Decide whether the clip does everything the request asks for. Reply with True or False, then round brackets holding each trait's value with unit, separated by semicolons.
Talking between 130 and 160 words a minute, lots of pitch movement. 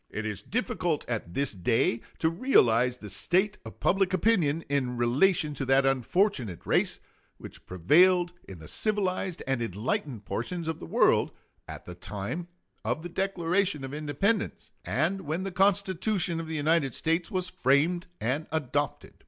True (155 wpm; 6.8 semitones)